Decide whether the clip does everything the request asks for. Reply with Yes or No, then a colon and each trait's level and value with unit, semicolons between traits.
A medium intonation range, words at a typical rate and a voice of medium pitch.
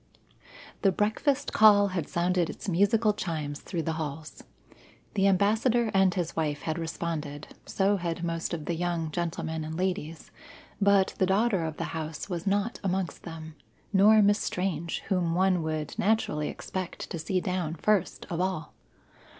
Yes: average, 3.5 semitones; average, 160 wpm; medium, 175 Hz